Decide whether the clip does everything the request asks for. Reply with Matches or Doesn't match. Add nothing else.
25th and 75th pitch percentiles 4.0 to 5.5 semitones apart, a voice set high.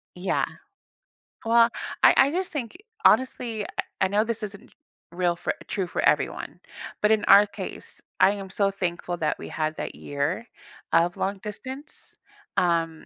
Matches